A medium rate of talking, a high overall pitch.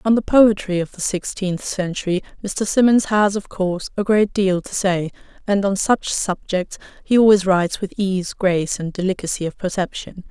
Yes: average, 180 wpm; high, 195 Hz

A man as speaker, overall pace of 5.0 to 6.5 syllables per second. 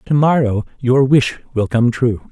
No: male; 4.3 syllables/s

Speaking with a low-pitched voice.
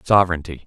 Yes: very low, 85 Hz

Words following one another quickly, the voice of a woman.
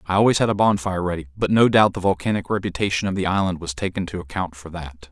No: fast, 245 wpm; male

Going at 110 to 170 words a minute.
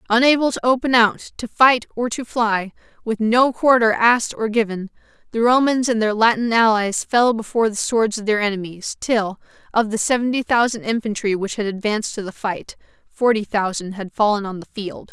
No: average, 185 wpm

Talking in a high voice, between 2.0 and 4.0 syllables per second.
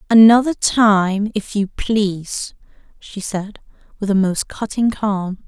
Yes: high, 205 Hz; 3.6 syllables/s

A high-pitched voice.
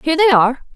Yes: very high, 290 Hz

